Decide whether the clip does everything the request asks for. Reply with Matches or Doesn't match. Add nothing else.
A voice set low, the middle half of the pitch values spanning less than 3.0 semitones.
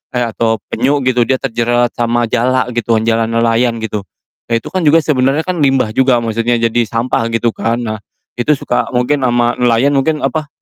Matches